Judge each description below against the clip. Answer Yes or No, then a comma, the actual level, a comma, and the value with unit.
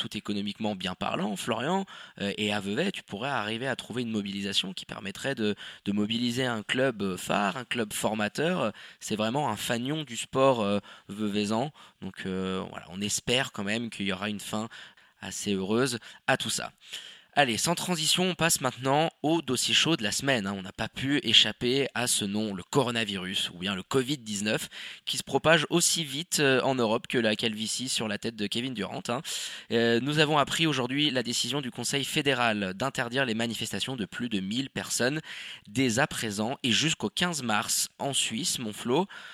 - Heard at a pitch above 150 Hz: No, low, 115 Hz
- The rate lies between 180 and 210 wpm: Yes, average, 185 wpm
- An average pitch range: Yes, average, 4.6 semitones